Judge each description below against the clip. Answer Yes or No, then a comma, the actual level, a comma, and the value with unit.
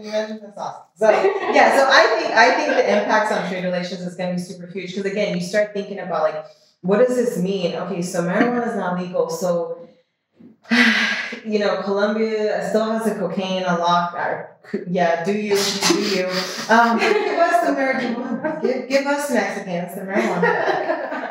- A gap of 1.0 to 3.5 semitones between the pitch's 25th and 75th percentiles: No, average, 4.1 semitones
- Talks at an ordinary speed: Yes, average, 175 wpm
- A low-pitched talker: No, high, 205 Hz